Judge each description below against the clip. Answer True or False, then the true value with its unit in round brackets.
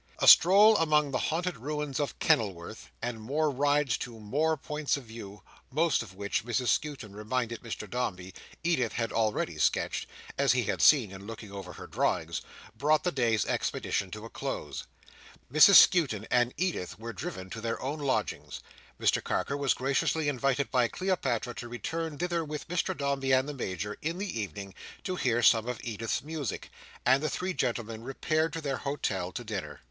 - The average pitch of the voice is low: True (130 Hz)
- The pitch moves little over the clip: False (5.4 semitones)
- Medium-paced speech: True (180 wpm)